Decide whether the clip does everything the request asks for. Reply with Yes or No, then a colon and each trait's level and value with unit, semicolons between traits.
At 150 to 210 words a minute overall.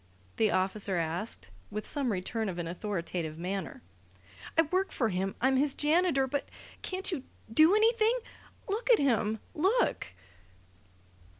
No: slow, 135 wpm